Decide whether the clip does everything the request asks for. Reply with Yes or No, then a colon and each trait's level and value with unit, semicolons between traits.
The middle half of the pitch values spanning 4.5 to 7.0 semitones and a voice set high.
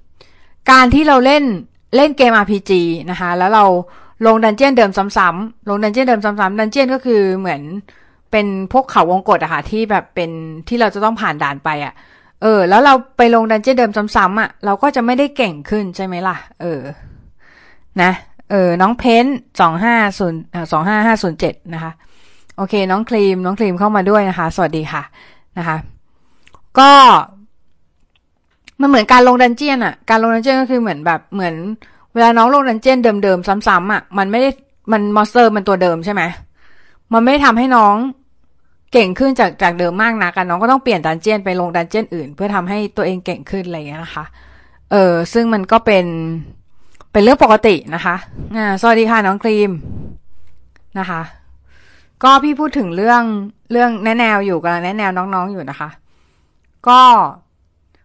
Yes: average, 5.0 semitones; high, 205 Hz